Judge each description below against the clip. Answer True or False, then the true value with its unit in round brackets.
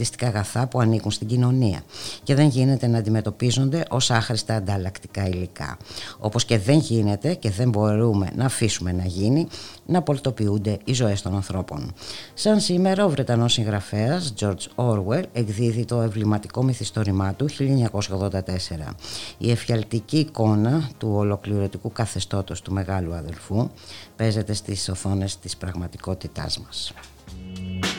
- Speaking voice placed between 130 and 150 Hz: False (110 Hz)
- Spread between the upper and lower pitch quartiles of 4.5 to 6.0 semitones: False (4.0 semitones)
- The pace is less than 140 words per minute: True (125 wpm)